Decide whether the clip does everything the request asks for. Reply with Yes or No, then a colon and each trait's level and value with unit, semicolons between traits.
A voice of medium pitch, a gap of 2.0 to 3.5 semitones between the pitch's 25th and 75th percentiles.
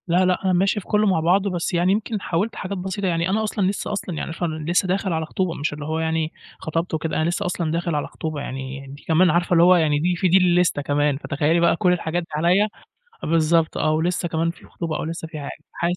Yes: medium, 170 Hz; narrow, 2.5 semitones